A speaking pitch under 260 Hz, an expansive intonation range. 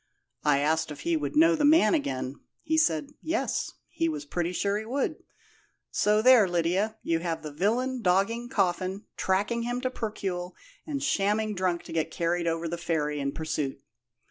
Yes: medium, 185 Hz; wide, 5.9 semitones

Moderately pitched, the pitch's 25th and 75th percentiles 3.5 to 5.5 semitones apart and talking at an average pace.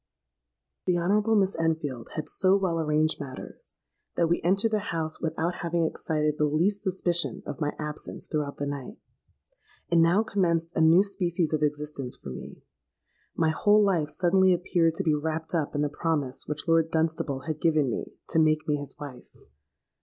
No: medium, 160 Hz; average, 2.7 semitones; average, 175 wpm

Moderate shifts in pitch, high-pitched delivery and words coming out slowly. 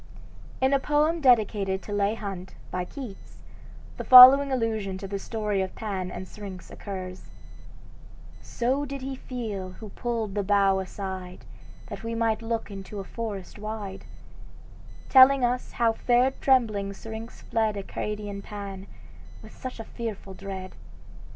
No: average, 3.6 semitones; high, 210 Hz; average, 145 wpm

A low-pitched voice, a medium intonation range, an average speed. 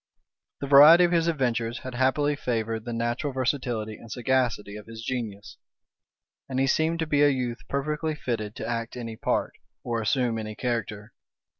Yes: low, 125 Hz; average, 3.6 semitones; average, 170 wpm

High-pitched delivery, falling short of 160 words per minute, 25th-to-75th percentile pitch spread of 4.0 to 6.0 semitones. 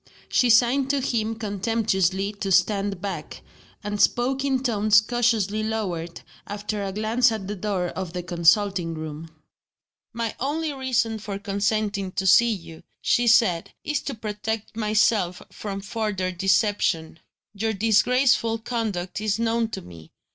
No: high, 210 Hz; average, 140 wpm; average, 3.1 semitones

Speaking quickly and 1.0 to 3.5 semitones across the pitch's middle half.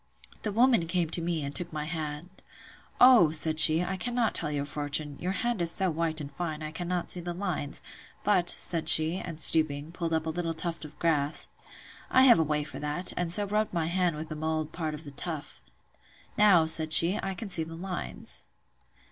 Yes: fast, 210 wpm; average, 2.7 semitones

